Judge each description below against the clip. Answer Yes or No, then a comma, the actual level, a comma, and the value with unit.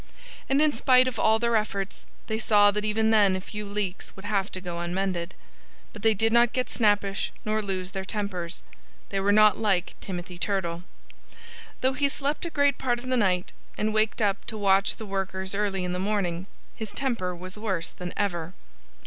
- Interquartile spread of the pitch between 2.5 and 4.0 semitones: Yes, average, 2.8 semitones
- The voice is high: Yes, high, 205 Hz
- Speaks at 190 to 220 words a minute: Yes, average, 195 wpm